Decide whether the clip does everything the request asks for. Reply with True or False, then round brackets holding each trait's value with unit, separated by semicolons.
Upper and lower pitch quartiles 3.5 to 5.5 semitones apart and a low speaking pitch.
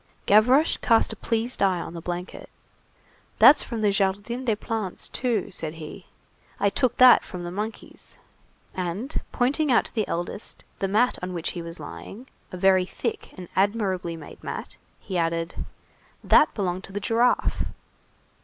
False (4.5 semitones; 195 Hz)